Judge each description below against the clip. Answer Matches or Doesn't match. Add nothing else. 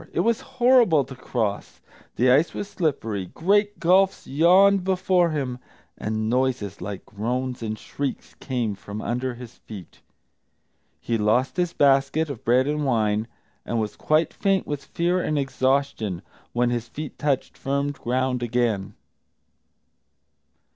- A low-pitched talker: Matches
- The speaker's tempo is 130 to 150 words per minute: Matches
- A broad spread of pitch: Matches